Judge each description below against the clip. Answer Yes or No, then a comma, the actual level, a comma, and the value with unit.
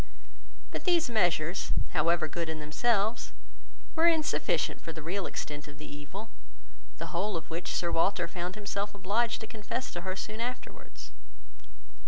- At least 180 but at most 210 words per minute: No, average, 155 wpm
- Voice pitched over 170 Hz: Yes, medium, 185 Hz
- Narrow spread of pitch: No, average, 5.0 semitones